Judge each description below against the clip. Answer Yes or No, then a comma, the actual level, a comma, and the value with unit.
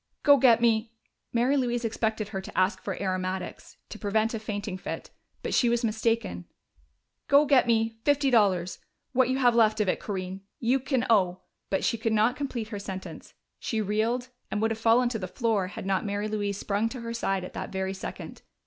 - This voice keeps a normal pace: No, fast, 210 wpm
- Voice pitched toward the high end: Yes, high, 220 Hz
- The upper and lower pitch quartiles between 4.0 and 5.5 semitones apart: No, average, 3.1 semitones